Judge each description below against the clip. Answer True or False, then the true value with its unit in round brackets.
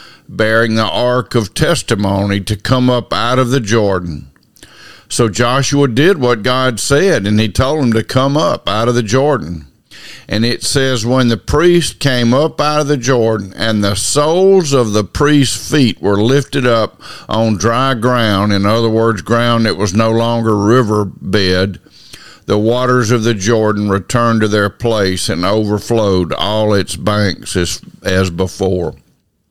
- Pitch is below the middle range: True (115 Hz)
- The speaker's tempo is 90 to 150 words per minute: False (165 wpm)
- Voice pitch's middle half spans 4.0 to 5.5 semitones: False (3.5 semitones)